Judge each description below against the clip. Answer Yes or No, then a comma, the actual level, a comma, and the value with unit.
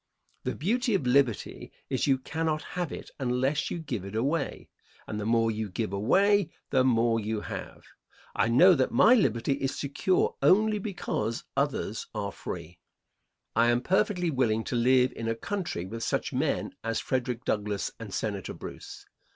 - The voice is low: Yes, low, 130 Hz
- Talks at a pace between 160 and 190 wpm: Yes, average, 165 wpm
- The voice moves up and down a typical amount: No, wide, 6.1 semitones